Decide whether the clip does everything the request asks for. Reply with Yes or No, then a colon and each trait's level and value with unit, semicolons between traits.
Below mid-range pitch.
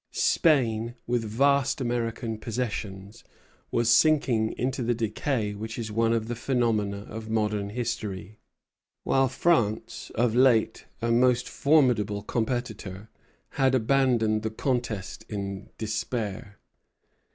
Yes: low, 115 Hz